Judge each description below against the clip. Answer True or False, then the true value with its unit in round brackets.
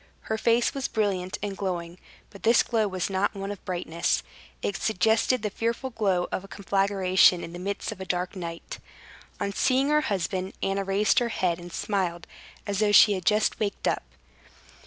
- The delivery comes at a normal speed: True (185 wpm)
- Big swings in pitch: False (2.9 semitones)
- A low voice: False (195 Hz)